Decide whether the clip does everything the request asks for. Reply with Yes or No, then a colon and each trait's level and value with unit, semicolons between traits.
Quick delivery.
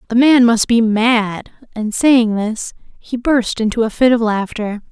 No: average, 185 wpm